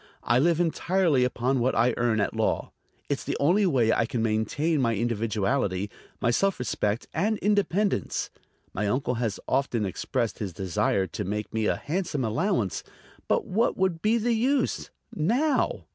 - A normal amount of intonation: No, wide, 8.8 semitones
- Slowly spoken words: No, average, 160 wpm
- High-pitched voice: No, low, 125 Hz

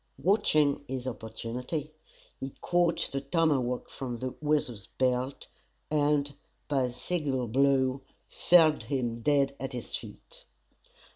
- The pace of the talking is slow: Yes, slow, 120 wpm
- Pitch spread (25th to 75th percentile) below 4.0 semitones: Yes, average, 3.0 semitones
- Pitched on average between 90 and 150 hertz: Yes, low, 135 Hz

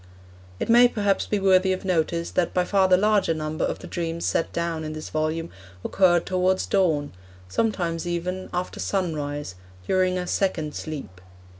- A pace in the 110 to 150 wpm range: No, average, 165 wpm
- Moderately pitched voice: Yes, medium, 175 Hz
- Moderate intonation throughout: Yes, average, 3.0 semitones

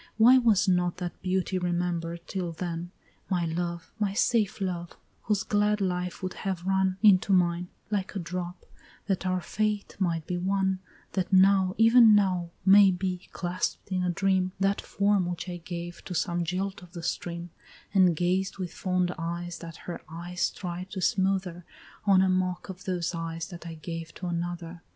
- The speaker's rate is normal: Yes, average, 175 wpm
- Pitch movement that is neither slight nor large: No, narrow, 1.7 semitones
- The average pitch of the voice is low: No, medium, 180 Hz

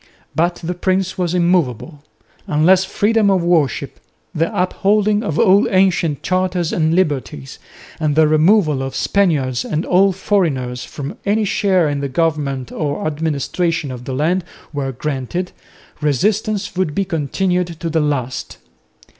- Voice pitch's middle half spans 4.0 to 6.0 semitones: Yes, average, 4.4 semitones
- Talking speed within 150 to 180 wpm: No, average, 140 wpm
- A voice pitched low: No, medium, 165 Hz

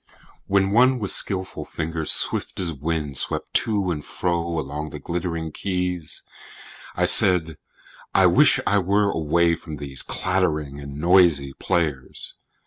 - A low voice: Yes, very low, 85 Hz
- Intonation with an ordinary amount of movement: Yes, average, 3.5 semitones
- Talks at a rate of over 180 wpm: No, slow, 135 wpm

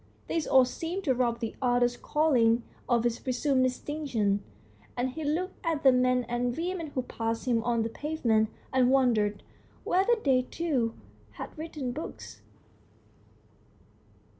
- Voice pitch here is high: Yes, very high, 255 Hz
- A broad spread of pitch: No, average, 4.3 semitones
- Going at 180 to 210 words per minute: No, average, 140 wpm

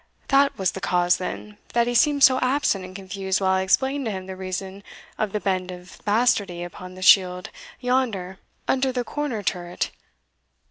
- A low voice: No, high, 195 Hz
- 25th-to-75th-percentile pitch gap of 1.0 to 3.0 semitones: No, average, 5.0 semitones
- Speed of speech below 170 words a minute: No, average, 180 wpm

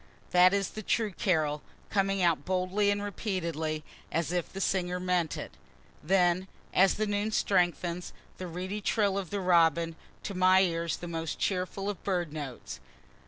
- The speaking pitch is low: No, medium, 180 Hz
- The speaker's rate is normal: Yes, average, 165 wpm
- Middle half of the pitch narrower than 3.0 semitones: Yes, narrow, 2.6 semitones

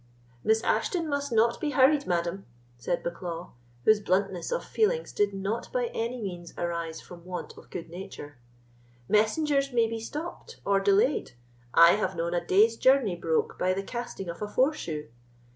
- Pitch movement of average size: No, wide, 6.9 semitones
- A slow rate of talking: No, average, 165 wpm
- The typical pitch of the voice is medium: No, high, 200 Hz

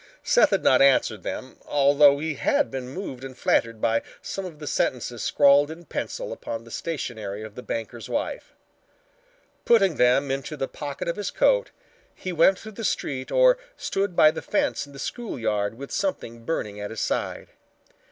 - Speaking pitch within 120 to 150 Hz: Yes, medium, 140 Hz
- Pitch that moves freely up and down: Yes, wide, 6.5 semitones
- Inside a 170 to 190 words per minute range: Yes, average, 180 wpm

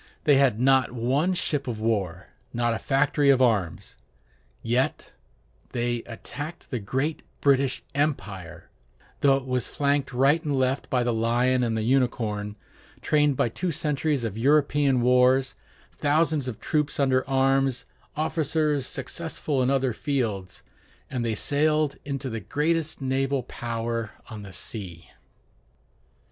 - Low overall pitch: Yes, low, 130 Hz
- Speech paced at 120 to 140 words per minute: Yes, slow, 135 wpm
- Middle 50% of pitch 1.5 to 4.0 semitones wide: Yes, average, 3.5 semitones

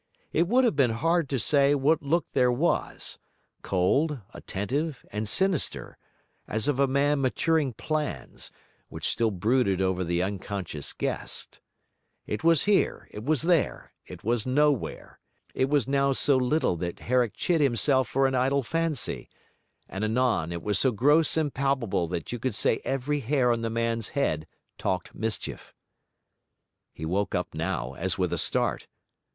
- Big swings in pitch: Yes, wide, 6.0 semitones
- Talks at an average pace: Yes, average, 160 wpm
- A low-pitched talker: Yes, low, 130 Hz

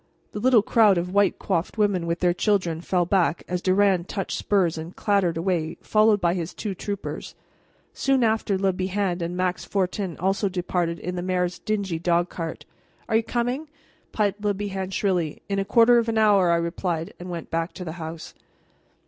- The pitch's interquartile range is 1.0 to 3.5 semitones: Yes, average, 2.9 semitones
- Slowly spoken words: No, average, 190 wpm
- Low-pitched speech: No, medium, 185 Hz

